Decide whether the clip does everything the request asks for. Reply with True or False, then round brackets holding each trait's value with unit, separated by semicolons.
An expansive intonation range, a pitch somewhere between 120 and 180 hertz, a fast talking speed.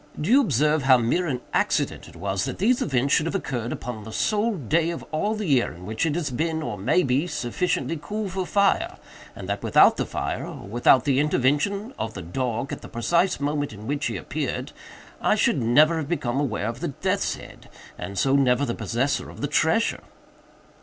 True (5.9 semitones; 140 Hz; 210 wpm)